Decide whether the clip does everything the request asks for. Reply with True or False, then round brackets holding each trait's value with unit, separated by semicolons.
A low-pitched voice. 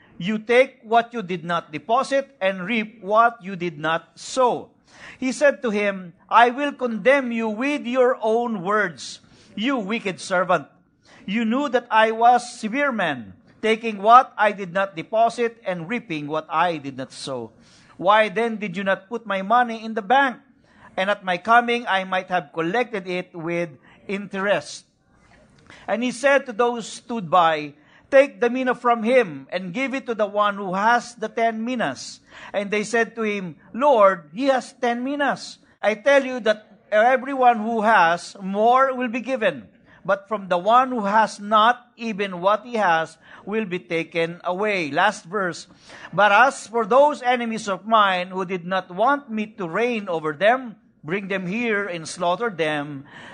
False (220 Hz)